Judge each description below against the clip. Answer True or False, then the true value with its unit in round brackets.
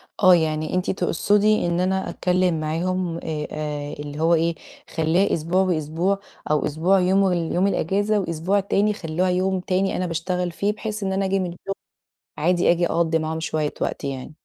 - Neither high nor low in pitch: True (180 Hz)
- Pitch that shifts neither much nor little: True (3.0 semitones)